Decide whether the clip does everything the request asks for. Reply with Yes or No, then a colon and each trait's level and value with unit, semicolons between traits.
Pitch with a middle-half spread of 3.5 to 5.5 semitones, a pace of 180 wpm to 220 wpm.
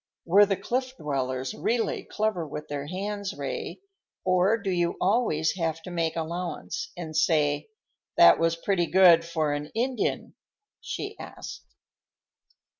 No: average, 4.3 semitones; slow, 135 wpm